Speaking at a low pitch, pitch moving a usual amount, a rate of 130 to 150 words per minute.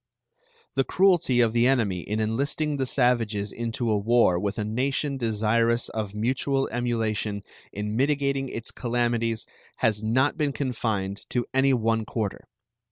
Yes: low, 115 Hz; average, 3.5 semitones; average, 145 wpm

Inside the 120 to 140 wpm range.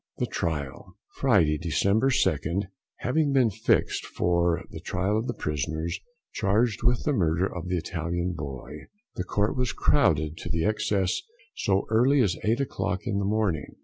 No: average, 155 wpm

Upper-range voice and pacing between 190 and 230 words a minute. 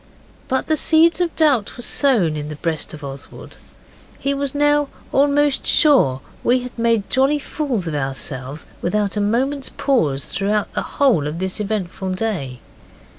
No: high, 220 Hz; average, 165 wpm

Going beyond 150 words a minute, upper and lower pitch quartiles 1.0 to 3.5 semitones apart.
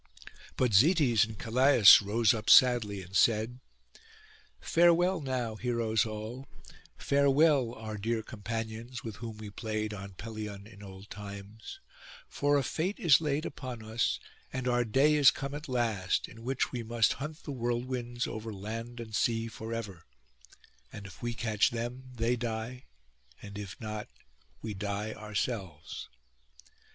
No: average, 145 wpm; average, 3.0 semitones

